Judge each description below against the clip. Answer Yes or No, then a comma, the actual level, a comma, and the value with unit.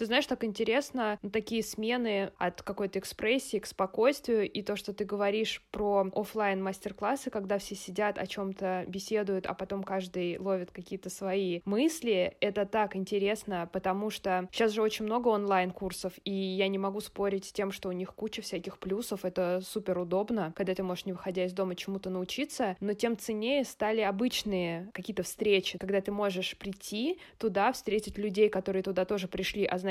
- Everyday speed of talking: No, fast, 180 wpm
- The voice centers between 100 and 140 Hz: No, high, 200 Hz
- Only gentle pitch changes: Yes, narrow, 2.2 semitones